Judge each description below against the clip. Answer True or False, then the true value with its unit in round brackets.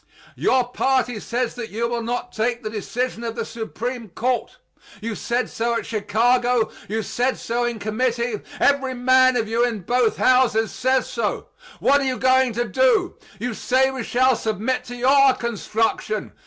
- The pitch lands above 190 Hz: True (240 Hz)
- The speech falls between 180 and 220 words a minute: False (170 wpm)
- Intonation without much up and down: True (2.3 semitones)